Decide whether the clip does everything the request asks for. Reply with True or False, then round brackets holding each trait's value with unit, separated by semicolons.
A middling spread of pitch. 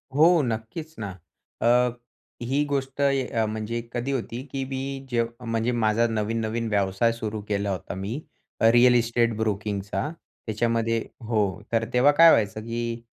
False (2.3 semitones)